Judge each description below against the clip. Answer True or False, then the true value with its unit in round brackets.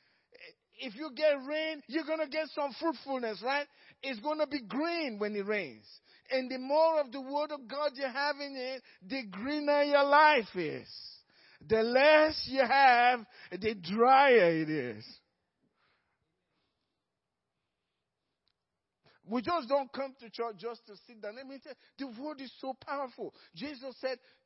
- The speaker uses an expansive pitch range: False (3.9 semitones)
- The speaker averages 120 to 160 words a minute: True (155 wpm)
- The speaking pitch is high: True (270 Hz)